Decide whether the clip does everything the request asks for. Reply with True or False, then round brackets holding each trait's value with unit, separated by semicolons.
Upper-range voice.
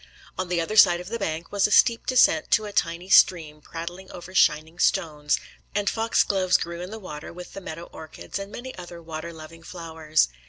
False (175 Hz)